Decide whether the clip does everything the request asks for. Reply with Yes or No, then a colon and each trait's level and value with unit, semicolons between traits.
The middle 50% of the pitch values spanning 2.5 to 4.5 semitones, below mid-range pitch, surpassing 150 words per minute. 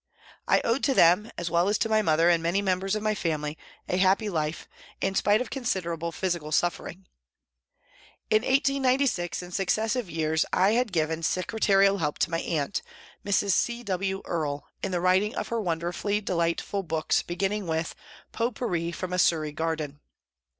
No: average, 4.0 semitones; medium, 185 Hz; average, 180 wpm